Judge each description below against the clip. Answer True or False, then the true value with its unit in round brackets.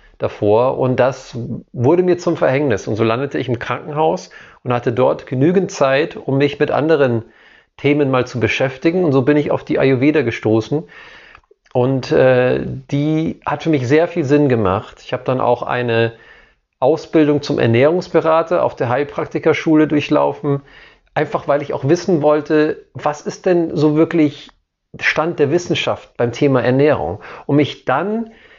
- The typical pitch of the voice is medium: True (145 Hz)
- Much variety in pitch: False (4.0 semitones)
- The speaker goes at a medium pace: True (160 wpm)